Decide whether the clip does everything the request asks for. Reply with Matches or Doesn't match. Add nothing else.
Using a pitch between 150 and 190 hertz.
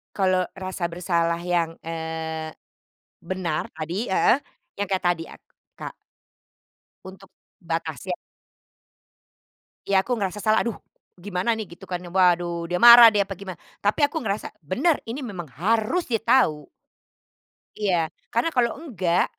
Matches